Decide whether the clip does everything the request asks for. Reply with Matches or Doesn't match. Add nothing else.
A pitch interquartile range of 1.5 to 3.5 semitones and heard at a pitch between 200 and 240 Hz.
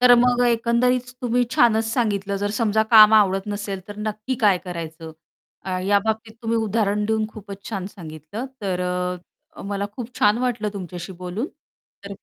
Matches